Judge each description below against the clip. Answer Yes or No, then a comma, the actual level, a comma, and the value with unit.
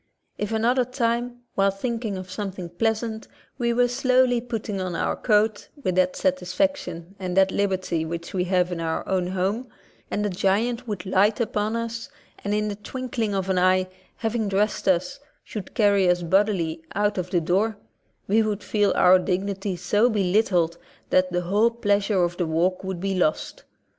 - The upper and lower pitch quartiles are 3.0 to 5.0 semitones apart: Yes, average, 3.3 semitones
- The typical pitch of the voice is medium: No, high, 195 Hz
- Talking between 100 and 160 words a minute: No, average, 180 wpm